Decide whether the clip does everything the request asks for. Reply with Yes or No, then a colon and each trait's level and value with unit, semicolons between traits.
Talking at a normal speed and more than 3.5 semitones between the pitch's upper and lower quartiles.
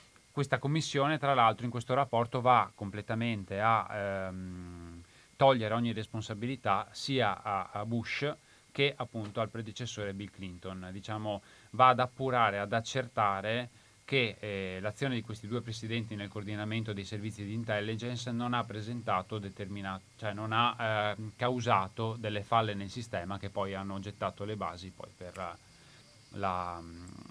No: average, 145 wpm; average, 3.0 semitones